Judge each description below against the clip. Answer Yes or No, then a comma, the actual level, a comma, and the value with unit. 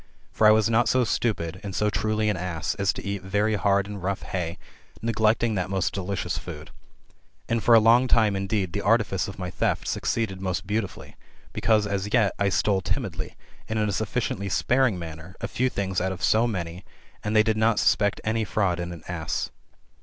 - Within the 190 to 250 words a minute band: Yes, average, 200 wpm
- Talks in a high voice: No, low, 100 Hz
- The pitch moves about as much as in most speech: Yes, average, 3.0 semitones